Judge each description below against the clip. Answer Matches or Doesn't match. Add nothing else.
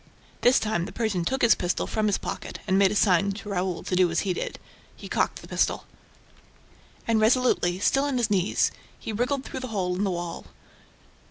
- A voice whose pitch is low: Doesn't match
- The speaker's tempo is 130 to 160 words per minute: Doesn't match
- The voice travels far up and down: Doesn't match